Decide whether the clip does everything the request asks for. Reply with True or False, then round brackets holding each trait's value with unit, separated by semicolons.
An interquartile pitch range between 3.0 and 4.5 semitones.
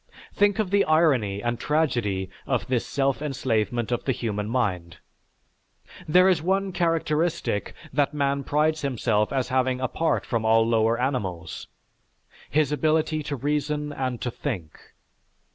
False (5.2 semitones)